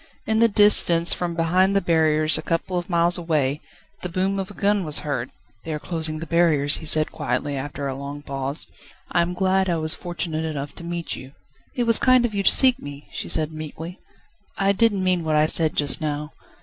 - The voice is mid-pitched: Yes, medium, 165 Hz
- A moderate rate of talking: No, fast, 220 wpm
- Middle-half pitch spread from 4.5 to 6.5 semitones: No, average, 3.7 semitones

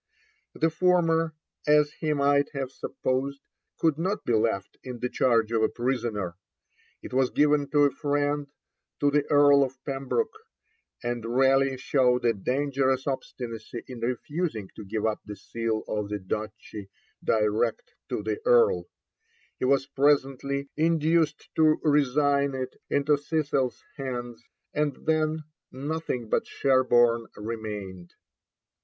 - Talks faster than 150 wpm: No, slow, 135 wpm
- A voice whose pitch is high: No, low, 135 Hz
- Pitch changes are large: No, average, 3.9 semitones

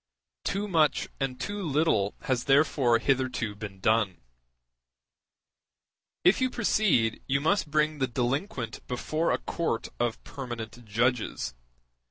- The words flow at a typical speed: No, slow, 120 wpm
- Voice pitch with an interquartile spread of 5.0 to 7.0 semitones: Yes, average, 5.3 semitones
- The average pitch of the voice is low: Yes, low, 130 Hz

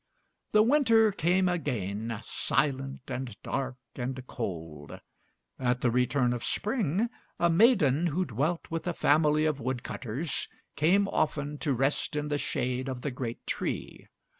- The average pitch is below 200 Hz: Yes, medium, 140 Hz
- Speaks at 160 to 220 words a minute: No, average, 145 wpm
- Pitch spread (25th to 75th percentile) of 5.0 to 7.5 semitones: Yes, average, 5.3 semitones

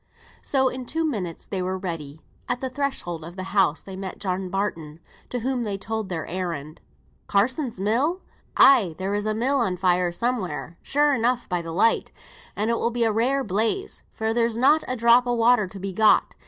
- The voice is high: Yes, high, 215 Hz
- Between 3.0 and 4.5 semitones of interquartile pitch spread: No, average, 5.1 semitones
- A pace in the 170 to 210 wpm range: Yes, average, 200 wpm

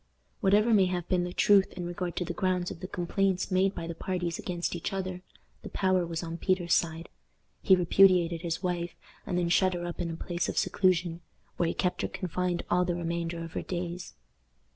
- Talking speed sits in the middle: No, fast, 210 wpm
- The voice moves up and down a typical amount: No, narrow, 1.4 semitones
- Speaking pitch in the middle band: Yes, medium, 175 Hz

